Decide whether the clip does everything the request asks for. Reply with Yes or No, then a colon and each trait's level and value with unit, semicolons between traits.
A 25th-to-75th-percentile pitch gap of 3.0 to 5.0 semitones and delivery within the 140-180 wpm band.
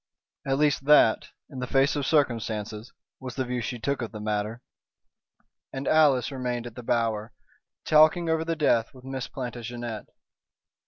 Yes: average, 3.3 semitones; average, 160 wpm